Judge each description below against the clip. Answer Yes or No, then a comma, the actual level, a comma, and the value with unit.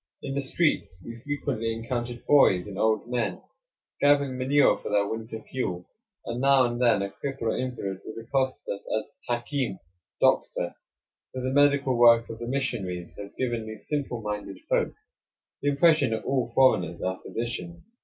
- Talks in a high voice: No, low, 120 Hz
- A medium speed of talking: Yes, average, 165 wpm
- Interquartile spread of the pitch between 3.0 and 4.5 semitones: Yes, average, 3.8 semitones